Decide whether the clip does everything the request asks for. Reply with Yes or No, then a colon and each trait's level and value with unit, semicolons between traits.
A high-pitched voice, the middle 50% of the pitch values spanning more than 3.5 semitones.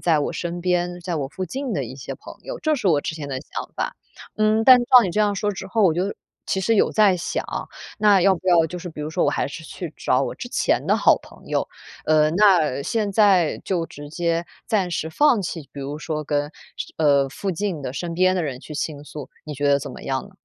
No: medium, 175 Hz; average, 4.7 semitones